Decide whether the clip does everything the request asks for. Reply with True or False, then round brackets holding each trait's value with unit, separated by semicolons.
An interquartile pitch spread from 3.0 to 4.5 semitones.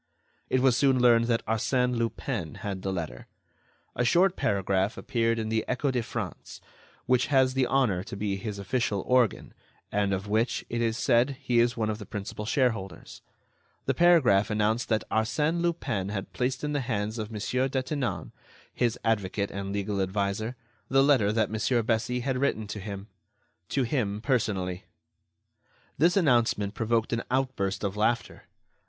True (3.9 semitones)